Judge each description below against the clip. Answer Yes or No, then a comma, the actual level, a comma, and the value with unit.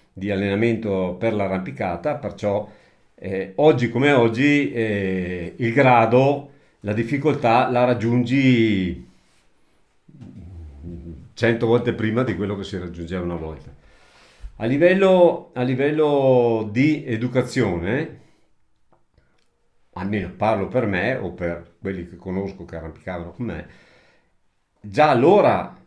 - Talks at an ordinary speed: No, slow, 110 wpm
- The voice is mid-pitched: No, low, 110 Hz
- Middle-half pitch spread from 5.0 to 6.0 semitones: Yes, wide, 5.4 semitones